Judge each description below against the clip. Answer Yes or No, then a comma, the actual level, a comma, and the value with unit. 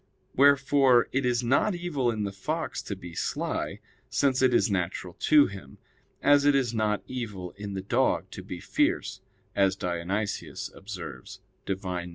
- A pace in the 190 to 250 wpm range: No, average, 165 wpm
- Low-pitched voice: Yes, low, 105 Hz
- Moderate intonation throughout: No, wide, 6.0 semitones